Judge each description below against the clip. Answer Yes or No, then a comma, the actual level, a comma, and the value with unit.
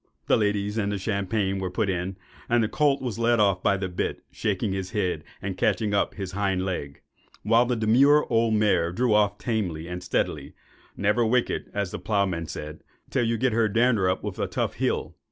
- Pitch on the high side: No, low, 105 Hz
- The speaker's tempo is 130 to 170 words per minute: No, fast, 205 wpm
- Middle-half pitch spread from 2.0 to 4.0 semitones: Yes, average, 3.3 semitones